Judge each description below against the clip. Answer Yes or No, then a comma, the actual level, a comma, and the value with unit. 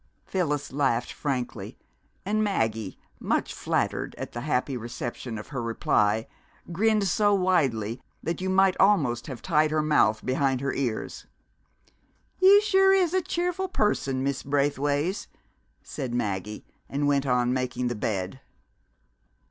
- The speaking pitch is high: No, medium, 140 Hz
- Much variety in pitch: Yes, wide, 7.7 semitones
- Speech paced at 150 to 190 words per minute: No, slow, 135 wpm